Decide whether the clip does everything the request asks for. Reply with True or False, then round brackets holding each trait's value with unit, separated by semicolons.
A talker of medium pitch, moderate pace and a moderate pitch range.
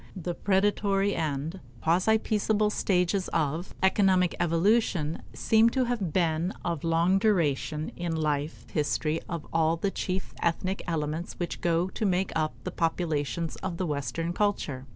True (175 Hz; 145 wpm; 3.4 semitones)